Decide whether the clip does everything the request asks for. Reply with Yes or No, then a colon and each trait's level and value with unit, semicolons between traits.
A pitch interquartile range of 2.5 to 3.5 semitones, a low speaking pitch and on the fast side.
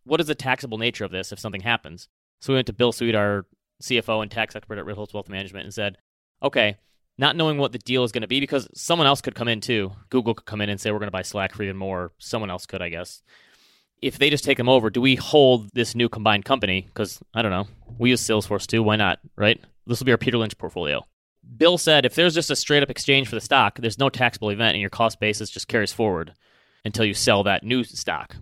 No: average, 3.9 semitones; low, 115 Hz; fast, 260 wpm